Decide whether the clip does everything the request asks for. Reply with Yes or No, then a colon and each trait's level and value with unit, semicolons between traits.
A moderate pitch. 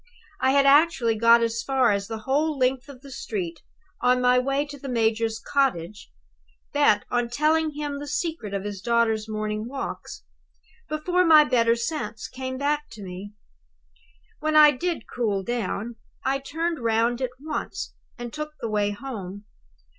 No: very high, 250 Hz